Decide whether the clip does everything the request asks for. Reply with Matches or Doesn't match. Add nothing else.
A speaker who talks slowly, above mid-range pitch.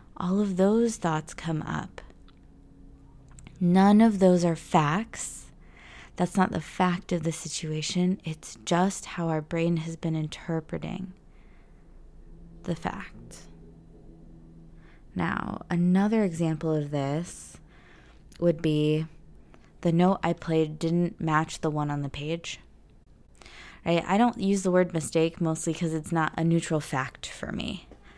Doesn't match